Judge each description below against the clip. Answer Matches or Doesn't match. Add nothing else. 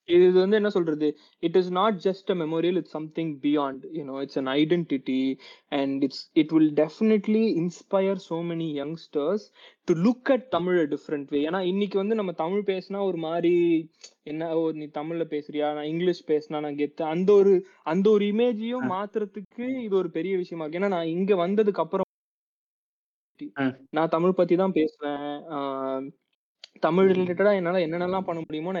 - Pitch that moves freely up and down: Doesn't match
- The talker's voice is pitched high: Doesn't match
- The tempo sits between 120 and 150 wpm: Matches